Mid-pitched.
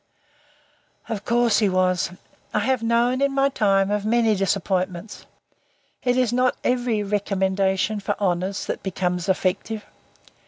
No: high, 205 Hz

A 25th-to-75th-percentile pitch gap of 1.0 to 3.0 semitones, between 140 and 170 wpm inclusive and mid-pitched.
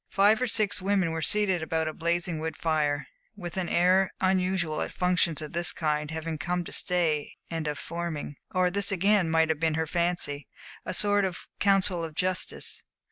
No: average, 2.7 semitones; average, 190 wpm; medium, 170 Hz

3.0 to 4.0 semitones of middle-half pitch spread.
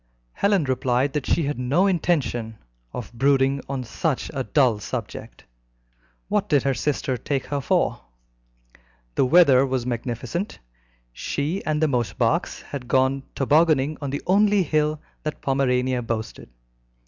Yes: average, 3.3 semitones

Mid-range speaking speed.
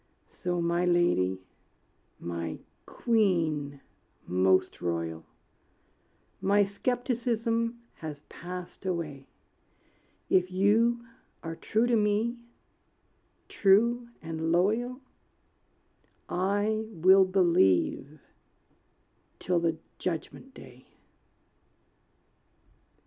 No: slow, 75 wpm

